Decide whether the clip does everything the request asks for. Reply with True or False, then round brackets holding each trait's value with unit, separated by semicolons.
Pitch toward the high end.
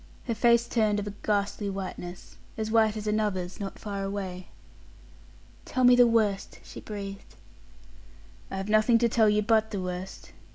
True (210 Hz)